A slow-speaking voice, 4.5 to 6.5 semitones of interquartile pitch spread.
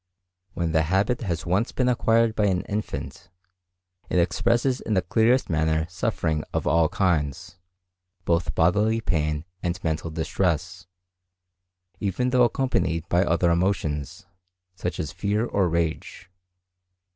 Yes: slow, 130 wpm; average, 4.8 semitones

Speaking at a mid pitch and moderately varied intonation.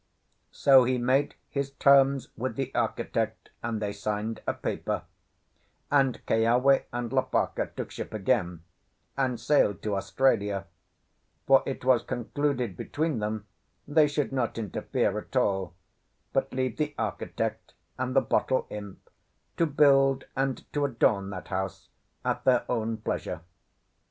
No: low, 125 Hz; average, 4.1 semitones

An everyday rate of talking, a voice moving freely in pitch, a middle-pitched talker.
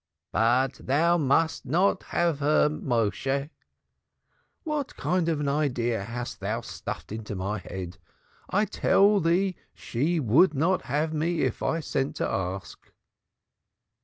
No: slow, 125 wpm; wide, 6.0 semitones; medium, 145 Hz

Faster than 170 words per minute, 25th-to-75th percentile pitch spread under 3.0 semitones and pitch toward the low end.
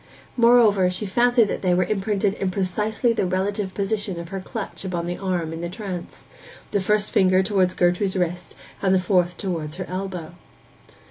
No: average, 180 wpm; narrow, 2.4 semitones; high, 190 Hz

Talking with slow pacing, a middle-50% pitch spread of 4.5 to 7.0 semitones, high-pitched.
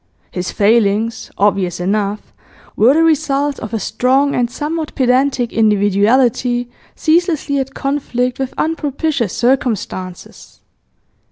Yes: slow, 105 wpm; average, 4.9 semitones; very high, 250 Hz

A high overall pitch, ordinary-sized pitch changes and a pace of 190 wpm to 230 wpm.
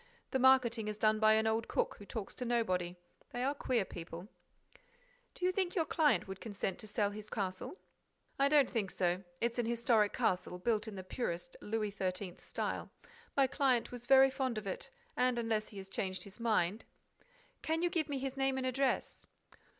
Yes: high, 225 Hz; average, 4.7 semitones; average, 195 wpm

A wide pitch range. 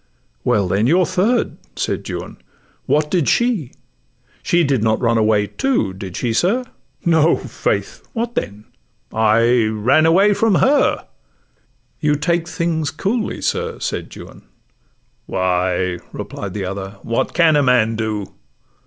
Yes: wide, 8.5 semitones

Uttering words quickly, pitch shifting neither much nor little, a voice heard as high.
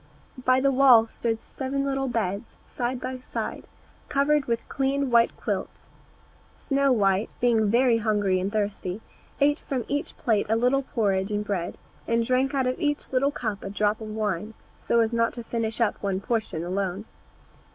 No: average, 170 wpm; average, 4.0 semitones; high, 230 Hz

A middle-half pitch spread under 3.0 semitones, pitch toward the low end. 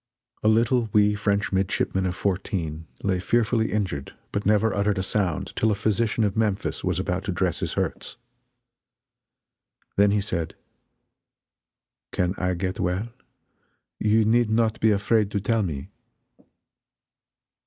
Yes: narrow, 2.6 semitones; low, 100 Hz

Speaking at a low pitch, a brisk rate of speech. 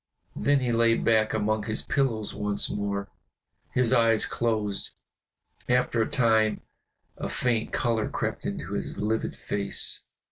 No: low, 110 Hz; slow, 135 wpm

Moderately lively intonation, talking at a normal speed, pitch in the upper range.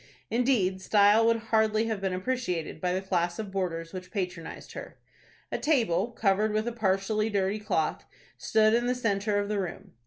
Yes: average, 3.0 semitones; average, 180 wpm; high, 205 Hz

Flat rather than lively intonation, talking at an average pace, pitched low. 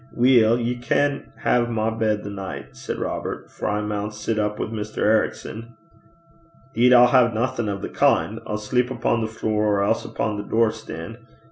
Yes: narrow, 2.1 semitones; average, 190 wpm; low, 110 Hz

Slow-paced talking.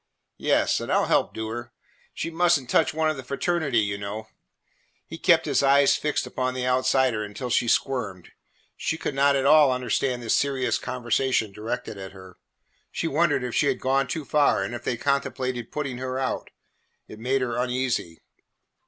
No: average, 190 wpm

